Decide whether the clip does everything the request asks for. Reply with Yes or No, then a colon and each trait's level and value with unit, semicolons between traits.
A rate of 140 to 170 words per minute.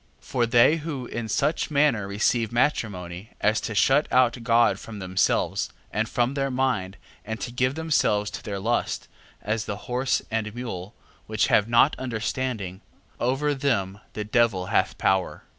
Yes: average, 160 wpm